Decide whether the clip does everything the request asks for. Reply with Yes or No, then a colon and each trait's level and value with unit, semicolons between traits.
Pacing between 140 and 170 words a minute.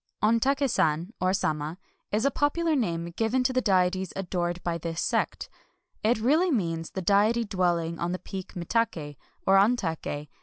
Yes: average, 160 wpm